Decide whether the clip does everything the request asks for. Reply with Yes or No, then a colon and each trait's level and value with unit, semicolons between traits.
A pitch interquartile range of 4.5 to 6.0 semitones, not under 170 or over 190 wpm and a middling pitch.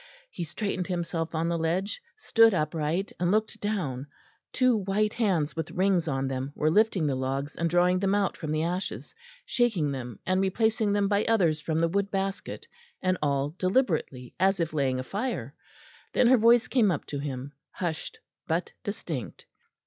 Yes: average, 5.0 semitones; average, 175 wpm; medium, 175 Hz